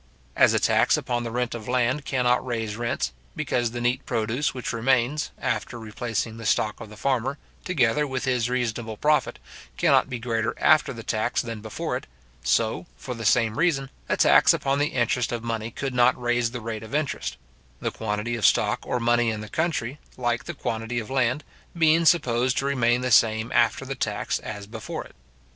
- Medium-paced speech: Yes, average, 195 wpm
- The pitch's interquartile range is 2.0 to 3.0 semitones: Yes, narrow, 2.5 semitones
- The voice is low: Yes, low, 120 Hz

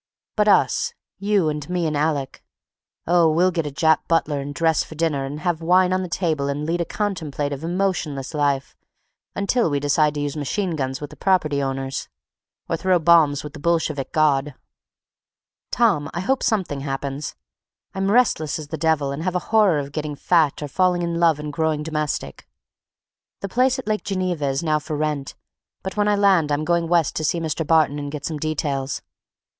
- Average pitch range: Yes, average, 3.5 semitones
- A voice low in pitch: No, medium, 155 Hz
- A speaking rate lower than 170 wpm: No, average, 185 wpm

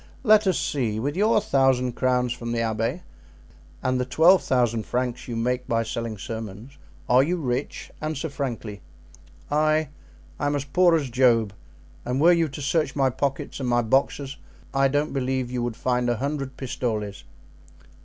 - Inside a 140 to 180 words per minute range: Yes, average, 170 wpm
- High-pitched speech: No, low, 130 Hz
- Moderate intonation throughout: Yes, average, 3.2 semitones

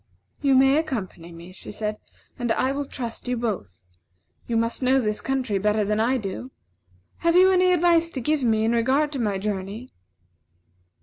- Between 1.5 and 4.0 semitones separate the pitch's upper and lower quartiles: No, average, 4.5 semitones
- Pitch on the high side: Yes, high, 240 Hz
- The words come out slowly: No, average, 180 wpm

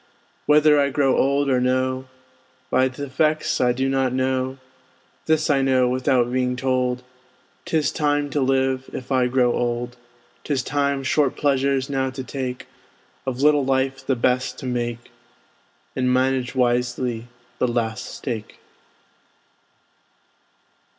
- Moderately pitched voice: No, low, 130 Hz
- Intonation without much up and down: Yes, narrow, 1.5 semitones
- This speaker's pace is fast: No, slow, 135 wpm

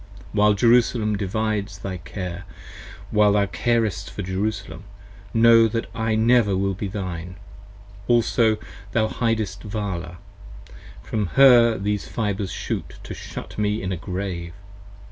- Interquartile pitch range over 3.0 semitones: No, average, 2.7 semitones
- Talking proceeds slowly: Yes, slow, 125 wpm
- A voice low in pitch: Yes, low, 105 Hz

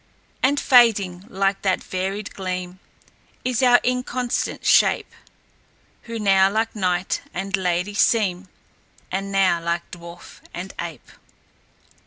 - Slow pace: Yes, slow, 115 wpm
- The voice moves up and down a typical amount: Yes, average, 3.3 semitones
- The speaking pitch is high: Yes, high, 195 Hz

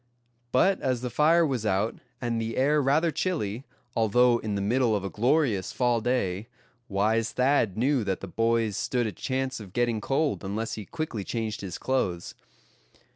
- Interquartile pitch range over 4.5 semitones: No, average, 4.0 semitones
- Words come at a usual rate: Yes, average, 175 wpm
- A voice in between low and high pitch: No, low, 115 Hz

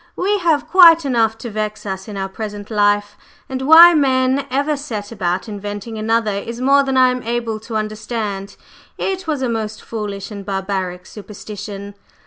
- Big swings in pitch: No, average, 4.3 semitones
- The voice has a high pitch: Yes, high, 220 Hz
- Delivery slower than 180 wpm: Yes, average, 170 wpm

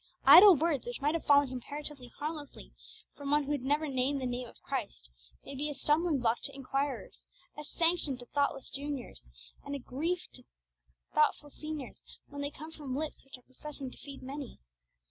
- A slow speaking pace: No, average, 185 wpm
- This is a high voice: Yes, very high, 285 Hz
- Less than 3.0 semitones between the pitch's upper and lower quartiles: Yes, narrow, 2.5 semitones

